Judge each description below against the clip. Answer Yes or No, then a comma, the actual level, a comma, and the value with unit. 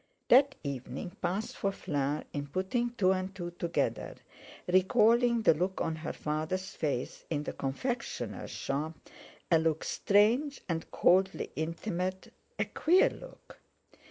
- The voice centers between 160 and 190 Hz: Yes, medium, 185 Hz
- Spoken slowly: Yes, slow, 130 wpm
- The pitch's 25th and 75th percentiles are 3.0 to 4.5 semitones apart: No, average, 5.2 semitones